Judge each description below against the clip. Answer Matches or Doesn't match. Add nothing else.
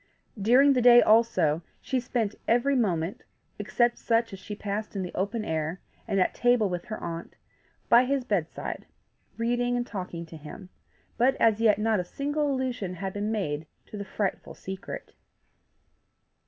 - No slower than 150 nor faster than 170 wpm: Matches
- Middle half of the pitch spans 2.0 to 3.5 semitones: Doesn't match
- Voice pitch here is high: Matches